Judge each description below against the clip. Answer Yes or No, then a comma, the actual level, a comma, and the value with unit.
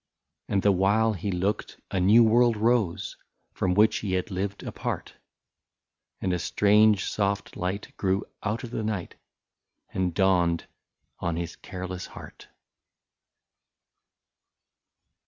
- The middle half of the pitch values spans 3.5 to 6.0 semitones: No, narrow, 2.6 semitones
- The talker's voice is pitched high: No, low, 100 Hz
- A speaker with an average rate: No, slow, 125 wpm